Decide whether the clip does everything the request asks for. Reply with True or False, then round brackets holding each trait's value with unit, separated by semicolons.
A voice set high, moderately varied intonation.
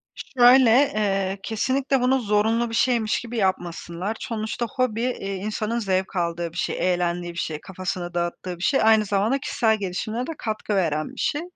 True (210 Hz; 4.6 semitones)